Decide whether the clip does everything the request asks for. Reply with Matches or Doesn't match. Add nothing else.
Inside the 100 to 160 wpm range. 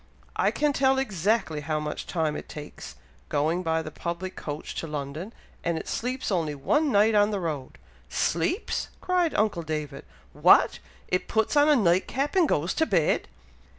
Doesn't match